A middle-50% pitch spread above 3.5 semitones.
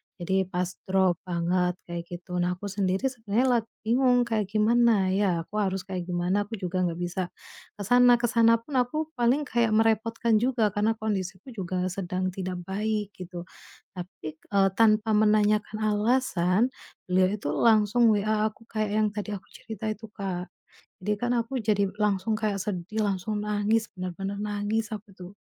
No: average, 3.1 semitones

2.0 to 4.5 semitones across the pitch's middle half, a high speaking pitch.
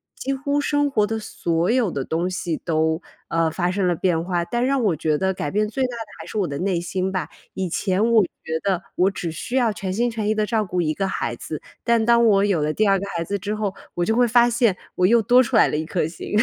No: average, 4.9 semitones; high, 195 Hz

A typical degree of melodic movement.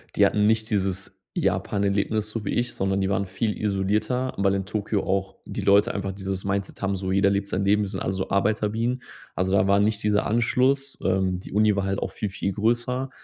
No: narrow, 2.0 semitones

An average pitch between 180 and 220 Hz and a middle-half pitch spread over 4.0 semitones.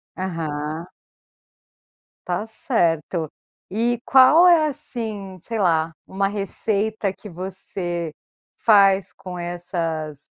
Yes: high, 190 Hz; average, 4.4 semitones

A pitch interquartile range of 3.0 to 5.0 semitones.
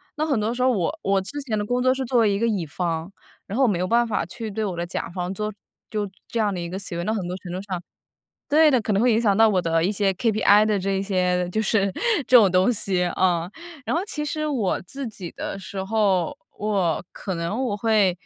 Yes: average, 3.8 semitones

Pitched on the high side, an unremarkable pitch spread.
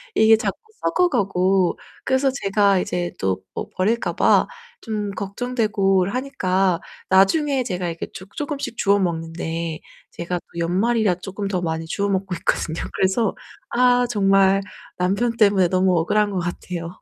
Yes: high, 195 Hz; average, 3.6 semitones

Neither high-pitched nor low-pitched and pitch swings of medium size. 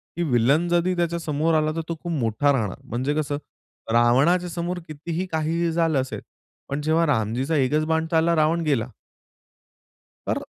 Yes: medium, 155 Hz; average, 3.6 semitones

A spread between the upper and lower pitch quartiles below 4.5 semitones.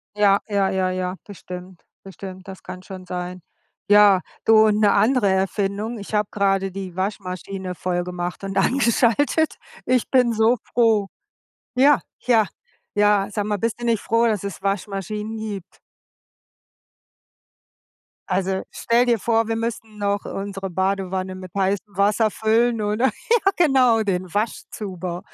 Yes: average, 2.9 semitones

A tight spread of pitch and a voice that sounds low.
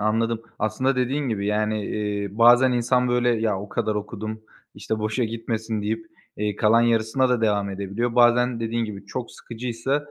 Yes: narrow, 2.3 semitones; low, 115 Hz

